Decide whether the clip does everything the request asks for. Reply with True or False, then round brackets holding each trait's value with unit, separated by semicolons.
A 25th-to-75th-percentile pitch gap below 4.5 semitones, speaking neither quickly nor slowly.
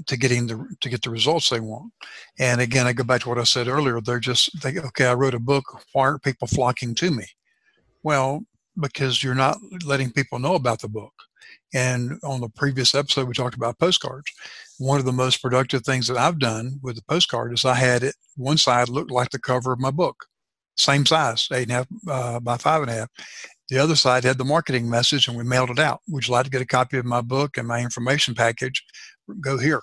False (2.4 semitones; 235 wpm)